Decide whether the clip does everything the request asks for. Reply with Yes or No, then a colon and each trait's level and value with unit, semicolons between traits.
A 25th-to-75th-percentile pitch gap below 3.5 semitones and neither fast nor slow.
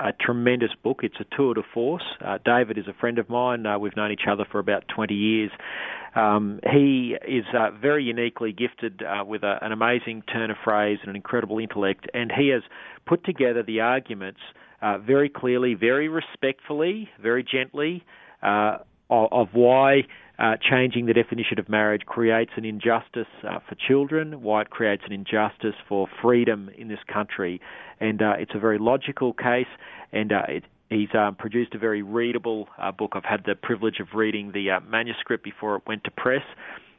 Yes: narrow, 2.6 semitones; average, 185 wpm